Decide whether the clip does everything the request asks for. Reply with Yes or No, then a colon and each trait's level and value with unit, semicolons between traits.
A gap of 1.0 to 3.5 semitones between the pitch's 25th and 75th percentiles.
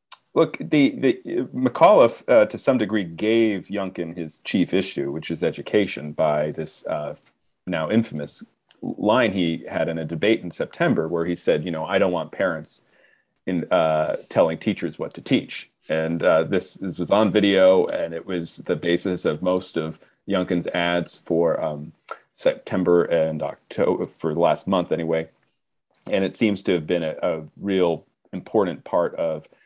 Yes: narrow, 2.4 semitones